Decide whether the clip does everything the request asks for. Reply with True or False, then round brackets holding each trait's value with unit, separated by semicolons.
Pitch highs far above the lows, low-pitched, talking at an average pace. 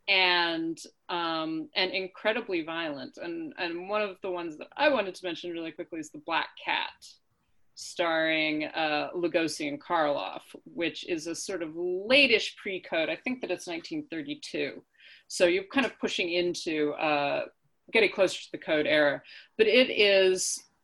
False (6.7 semitones; 180 Hz; 160 wpm)